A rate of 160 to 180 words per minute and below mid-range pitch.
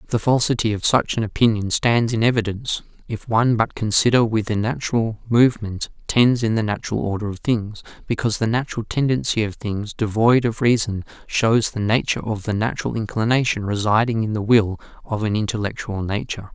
Yes: average, 170 wpm; low, 110 Hz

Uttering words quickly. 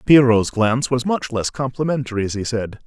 No: average, 190 wpm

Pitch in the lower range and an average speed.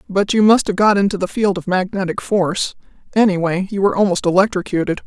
No: high, 190 Hz; average, 190 wpm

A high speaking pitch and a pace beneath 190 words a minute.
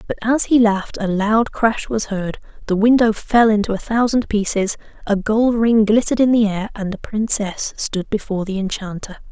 No: high, 215 Hz; average, 195 wpm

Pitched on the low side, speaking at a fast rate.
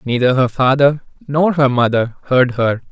No: low, 130 Hz; average, 165 wpm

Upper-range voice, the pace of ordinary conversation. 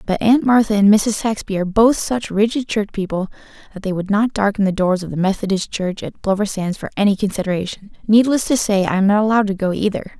No: high, 205 Hz; fast, 230 wpm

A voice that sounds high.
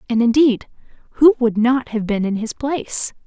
Yes: high, 240 Hz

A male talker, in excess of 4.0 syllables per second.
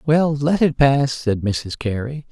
No: male; 3.8 syllables/s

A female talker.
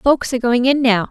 Yes: female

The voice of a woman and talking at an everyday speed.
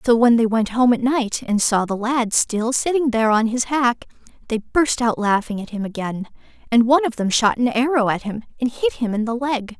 No: female; fast, 240 wpm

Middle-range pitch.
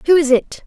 No: very high, 300 Hz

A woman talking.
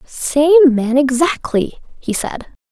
Yes: female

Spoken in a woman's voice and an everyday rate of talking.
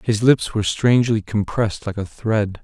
No: male; average, 180 wpm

